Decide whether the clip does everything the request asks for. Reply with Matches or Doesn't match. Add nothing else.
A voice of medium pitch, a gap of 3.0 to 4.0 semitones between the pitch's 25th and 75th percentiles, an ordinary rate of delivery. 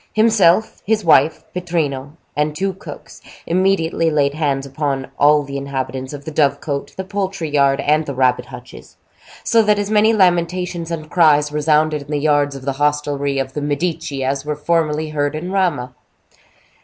Matches